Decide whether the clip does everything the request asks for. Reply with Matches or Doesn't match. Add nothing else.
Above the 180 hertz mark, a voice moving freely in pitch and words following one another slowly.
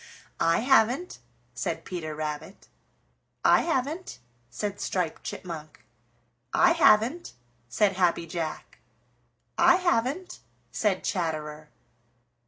Matches